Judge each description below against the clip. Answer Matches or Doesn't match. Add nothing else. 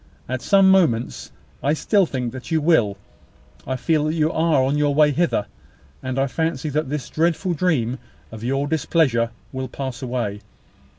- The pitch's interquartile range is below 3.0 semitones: Doesn't match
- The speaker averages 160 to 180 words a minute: Matches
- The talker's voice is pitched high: Doesn't match